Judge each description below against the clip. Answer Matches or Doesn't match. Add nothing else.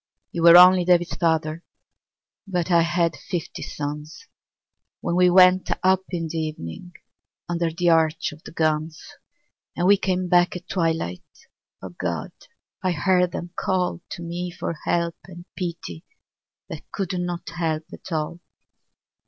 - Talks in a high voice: Doesn't match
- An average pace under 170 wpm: Matches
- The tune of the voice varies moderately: Doesn't match